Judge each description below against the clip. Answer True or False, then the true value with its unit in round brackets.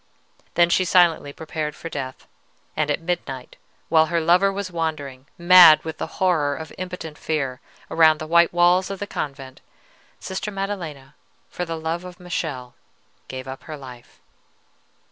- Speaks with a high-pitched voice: False (160 Hz)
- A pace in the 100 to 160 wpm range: True (150 wpm)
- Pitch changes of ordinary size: True (3.7 semitones)